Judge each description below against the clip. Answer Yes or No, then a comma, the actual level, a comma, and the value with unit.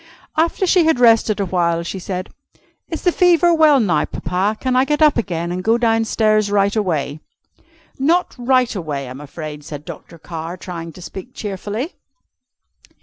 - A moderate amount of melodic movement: No, wide, 7.0 semitones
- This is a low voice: No, high, 205 Hz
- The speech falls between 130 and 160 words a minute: No, average, 170 wpm